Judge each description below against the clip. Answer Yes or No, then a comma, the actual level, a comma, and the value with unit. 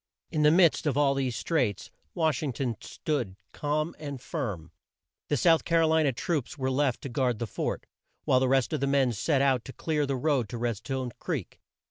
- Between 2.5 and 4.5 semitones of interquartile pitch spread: Yes, average, 3.4 semitones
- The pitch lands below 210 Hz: Yes, low, 135 Hz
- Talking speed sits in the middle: No, fast, 215 wpm